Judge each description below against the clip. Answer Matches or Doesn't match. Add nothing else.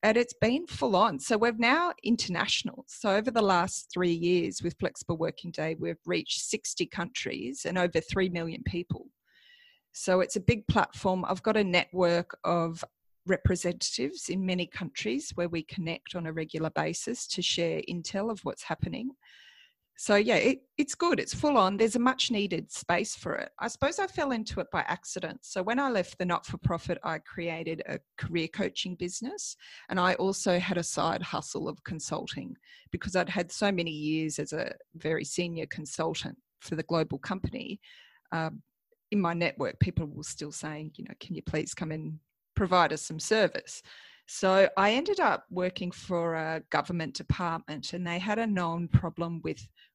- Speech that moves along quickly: Doesn't match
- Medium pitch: Matches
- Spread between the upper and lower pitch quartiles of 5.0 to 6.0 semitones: Matches